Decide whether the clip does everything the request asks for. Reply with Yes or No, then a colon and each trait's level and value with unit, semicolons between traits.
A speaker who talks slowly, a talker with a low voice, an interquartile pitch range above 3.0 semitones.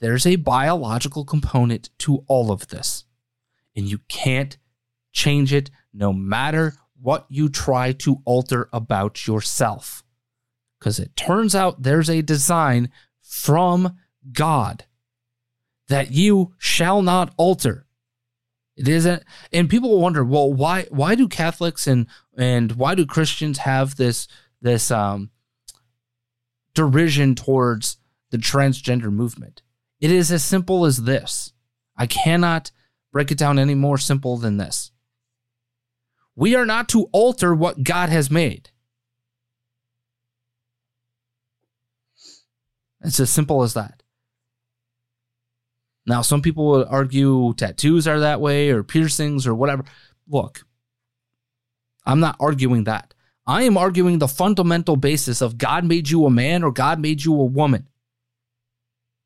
Yes: slow, 130 wpm; low, 130 Hz; average, 4.0 semitones